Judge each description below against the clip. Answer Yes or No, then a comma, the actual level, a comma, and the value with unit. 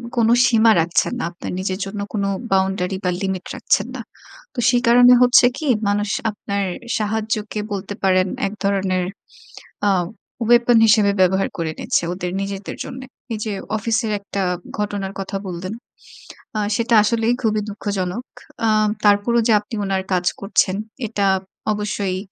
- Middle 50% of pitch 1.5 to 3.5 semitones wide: Yes, narrow, 2.5 semitones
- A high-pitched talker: Yes, high, 205 Hz